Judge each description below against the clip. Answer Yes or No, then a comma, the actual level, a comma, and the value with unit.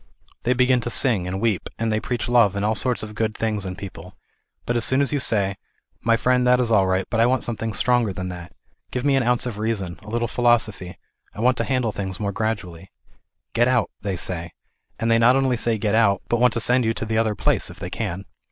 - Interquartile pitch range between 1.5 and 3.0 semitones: No, average, 3.5 semitones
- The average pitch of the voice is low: Yes, low, 115 Hz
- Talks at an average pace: No, fast, 255 wpm